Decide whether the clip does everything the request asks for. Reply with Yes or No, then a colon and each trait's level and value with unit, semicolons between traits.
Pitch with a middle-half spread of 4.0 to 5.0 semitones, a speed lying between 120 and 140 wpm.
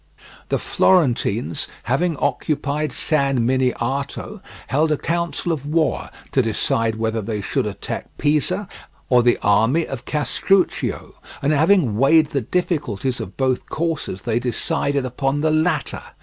Yes: average, 4.4 semitones; slow, 135 wpm